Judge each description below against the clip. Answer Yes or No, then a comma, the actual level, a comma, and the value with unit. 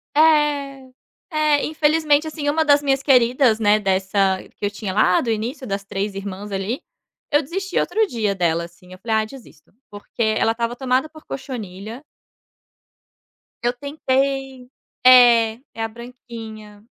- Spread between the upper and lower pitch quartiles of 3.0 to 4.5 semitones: No, wide, 5.4 semitones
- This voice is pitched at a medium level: No, high, 240 Hz